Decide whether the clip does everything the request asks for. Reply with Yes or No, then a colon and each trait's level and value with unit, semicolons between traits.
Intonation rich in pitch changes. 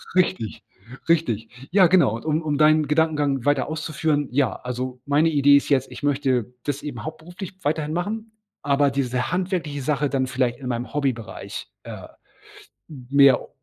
No: average, 3.4 semitones